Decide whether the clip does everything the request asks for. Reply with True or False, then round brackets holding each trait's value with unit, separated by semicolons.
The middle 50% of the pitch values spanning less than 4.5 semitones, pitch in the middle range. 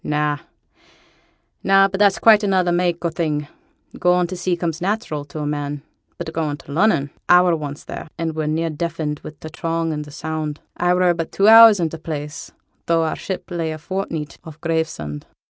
True (2.9 semitones; 165 Hz)